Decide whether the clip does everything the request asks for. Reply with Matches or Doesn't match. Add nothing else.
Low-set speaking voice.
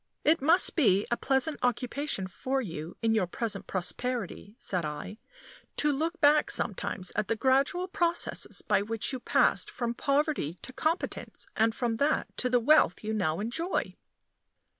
Doesn't match